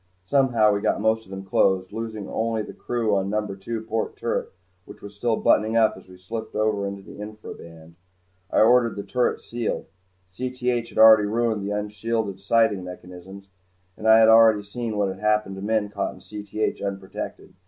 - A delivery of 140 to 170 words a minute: No, average, 185 wpm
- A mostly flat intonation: Yes, narrow, 2.3 semitones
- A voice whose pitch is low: Yes, low, 105 Hz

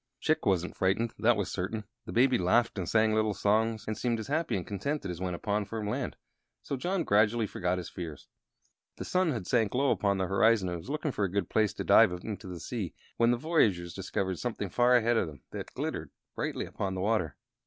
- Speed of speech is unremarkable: No, fast, 220 wpm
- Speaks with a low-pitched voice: Yes, low, 105 Hz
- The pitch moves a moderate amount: Yes, average, 4.1 semitones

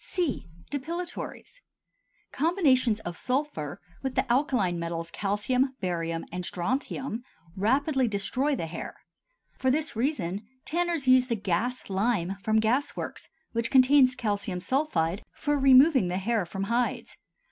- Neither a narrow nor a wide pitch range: No, wide, 6.0 semitones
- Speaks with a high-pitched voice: Yes, high, 240 Hz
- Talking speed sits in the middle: No, slow, 130 wpm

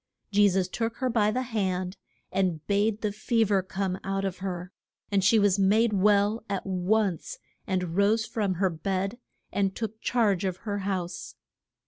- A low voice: No, high, 200 Hz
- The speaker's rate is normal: Yes, average, 170 wpm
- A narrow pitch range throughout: Yes, narrow, 2.3 semitones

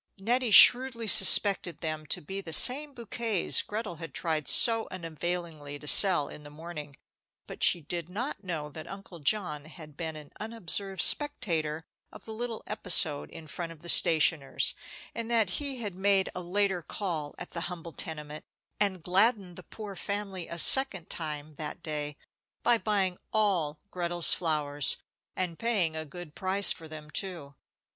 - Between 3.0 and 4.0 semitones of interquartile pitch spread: No, average, 4.6 semitones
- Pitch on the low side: No, medium, 175 Hz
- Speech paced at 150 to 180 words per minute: Yes, average, 165 wpm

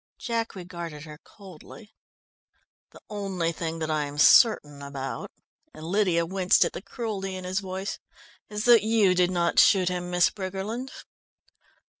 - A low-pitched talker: No, medium, 185 Hz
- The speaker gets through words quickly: No, average, 150 wpm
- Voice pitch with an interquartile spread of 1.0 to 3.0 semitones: No, average, 3.6 semitones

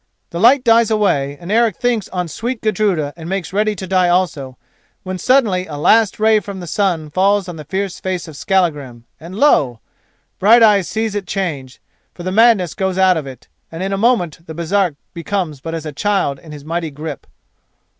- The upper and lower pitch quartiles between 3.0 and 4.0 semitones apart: No, average, 4.4 semitones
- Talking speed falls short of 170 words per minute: No, average, 195 wpm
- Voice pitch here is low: No, medium, 185 Hz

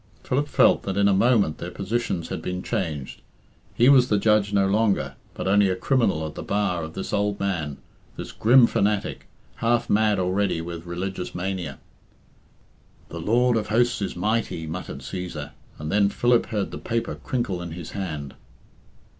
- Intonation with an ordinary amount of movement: Yes, average, 4.0 semitones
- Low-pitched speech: Yes, low, 100 Hz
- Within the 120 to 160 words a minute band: No, average, 170 wpm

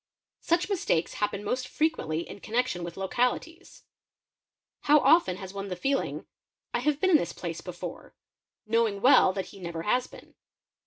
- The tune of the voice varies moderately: No, wide, 7.5 semitones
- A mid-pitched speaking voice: No, high, 230 Hz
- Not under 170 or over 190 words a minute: No, average, 160 wpm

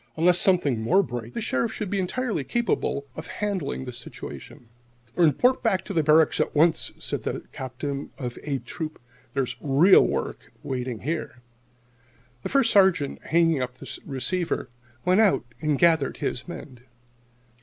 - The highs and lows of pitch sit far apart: Yes, wide, 5.9 semitones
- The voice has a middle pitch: Yes, medium, 155 Hz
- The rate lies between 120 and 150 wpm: No, average, 165 wpm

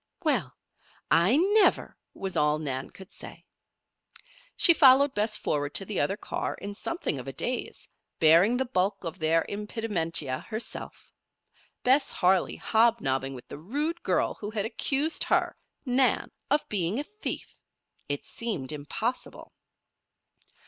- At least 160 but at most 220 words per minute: No, slow, 135 wpm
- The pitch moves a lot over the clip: Yes, wide, 8.0 semitones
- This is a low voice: No, high, 205 Hz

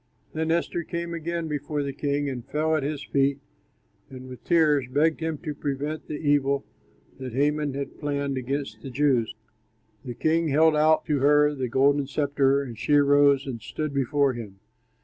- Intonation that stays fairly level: Yes, narrow, 2.0 semitones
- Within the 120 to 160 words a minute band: No, average, 175 wpm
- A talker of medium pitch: Yes, medium, 145 Hz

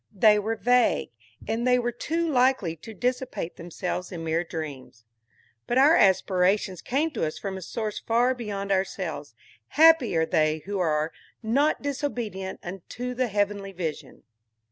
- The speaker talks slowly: No, average, 150 wpm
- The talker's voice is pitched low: No, high, 205 Hz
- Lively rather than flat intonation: Yes, wide, 6.0 semitones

